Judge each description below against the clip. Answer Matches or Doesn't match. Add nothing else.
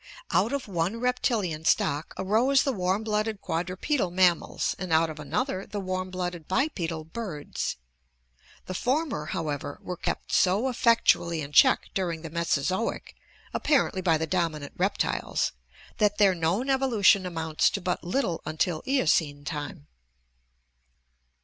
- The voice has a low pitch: Doesn't match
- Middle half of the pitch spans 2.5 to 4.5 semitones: Doesn't match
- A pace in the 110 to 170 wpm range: Matches